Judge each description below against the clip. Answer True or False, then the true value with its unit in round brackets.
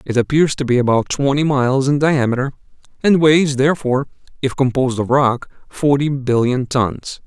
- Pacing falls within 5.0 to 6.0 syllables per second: True (5.3 syllables/s)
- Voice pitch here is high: False (135 Hz)